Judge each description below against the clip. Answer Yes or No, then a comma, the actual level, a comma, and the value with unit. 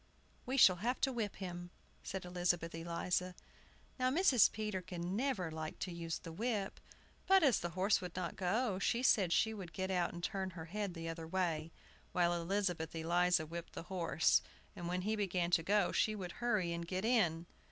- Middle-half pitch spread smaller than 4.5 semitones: Yes, average, 3.3 semitones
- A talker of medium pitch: Yes, medium, 180 Hz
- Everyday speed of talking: Yes, average, 190 wpm